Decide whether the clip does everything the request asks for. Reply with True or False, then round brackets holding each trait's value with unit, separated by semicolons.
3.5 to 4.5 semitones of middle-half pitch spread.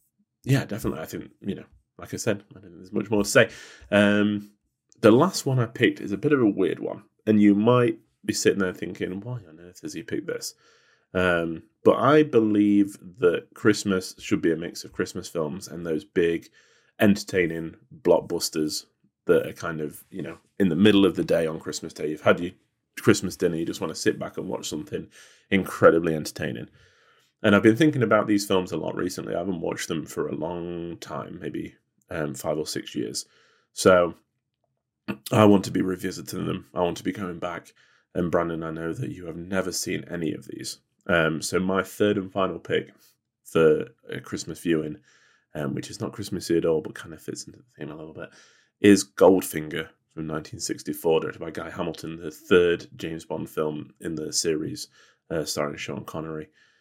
True (4.1 semitones)